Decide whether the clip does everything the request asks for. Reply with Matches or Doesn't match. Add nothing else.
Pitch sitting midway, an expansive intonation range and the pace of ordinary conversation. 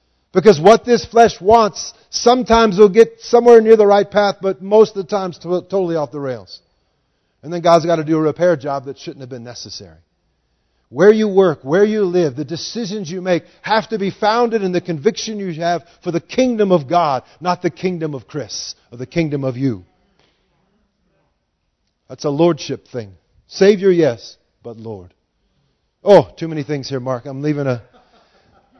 Matches